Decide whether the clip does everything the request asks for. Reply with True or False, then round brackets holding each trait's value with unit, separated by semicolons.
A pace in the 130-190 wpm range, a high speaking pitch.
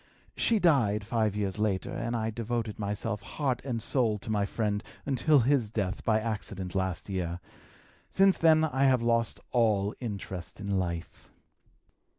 False (155 wpm; 110 Hz)